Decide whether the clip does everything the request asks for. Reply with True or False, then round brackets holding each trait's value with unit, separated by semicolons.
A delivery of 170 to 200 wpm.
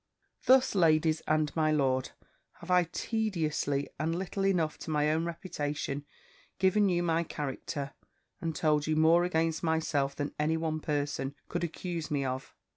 False (155 wpm)